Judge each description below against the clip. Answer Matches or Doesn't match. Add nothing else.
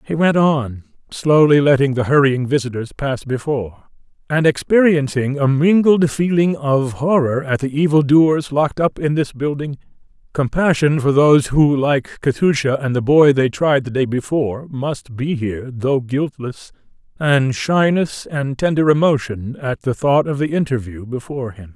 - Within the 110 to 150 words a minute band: Doesn't match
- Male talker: Matches